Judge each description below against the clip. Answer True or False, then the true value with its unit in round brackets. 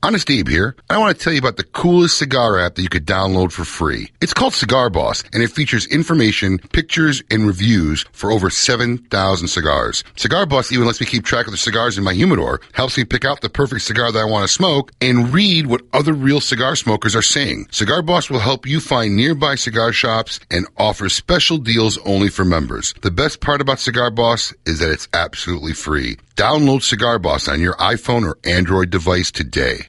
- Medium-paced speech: False (210 wpm)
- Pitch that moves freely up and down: True (5.9 semitones)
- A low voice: True (115 Hz)